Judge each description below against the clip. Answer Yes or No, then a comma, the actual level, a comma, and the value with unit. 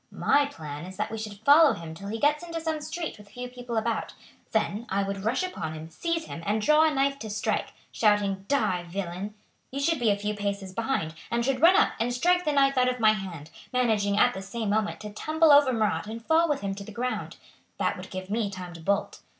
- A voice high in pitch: Yes, high, 220 Hz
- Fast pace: Yes, fast, 240 wpm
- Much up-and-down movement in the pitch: Yes, wide, 5.8 semitones